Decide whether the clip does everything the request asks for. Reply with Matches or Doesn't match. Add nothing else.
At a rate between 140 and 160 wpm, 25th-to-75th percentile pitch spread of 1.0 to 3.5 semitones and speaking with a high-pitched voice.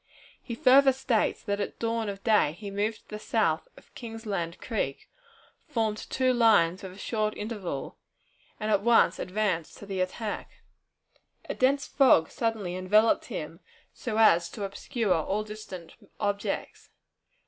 Matches